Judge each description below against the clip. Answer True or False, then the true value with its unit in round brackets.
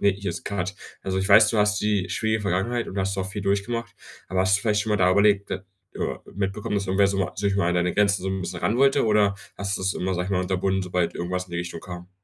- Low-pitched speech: True (100 Hz)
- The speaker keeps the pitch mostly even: True (1.9 semitones)